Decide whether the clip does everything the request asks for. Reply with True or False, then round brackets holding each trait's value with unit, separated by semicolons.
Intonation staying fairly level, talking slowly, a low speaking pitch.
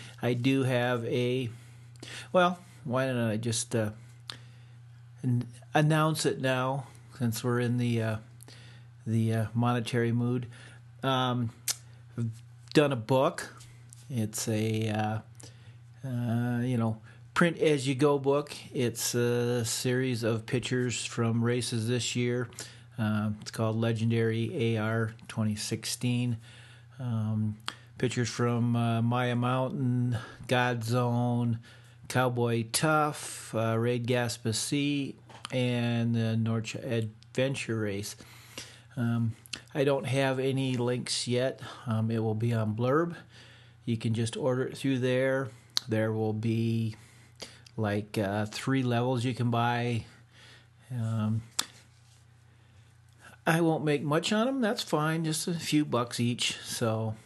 True (1.6 semitones; 125 wpm; 120 Hz)